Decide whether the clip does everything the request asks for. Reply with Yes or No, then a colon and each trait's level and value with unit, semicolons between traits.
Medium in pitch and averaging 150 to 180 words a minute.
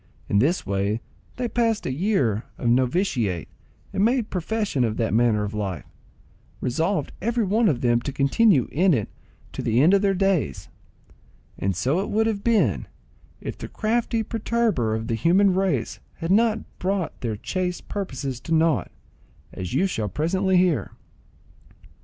Yes: medium, 165 Hz; average, 160 wpm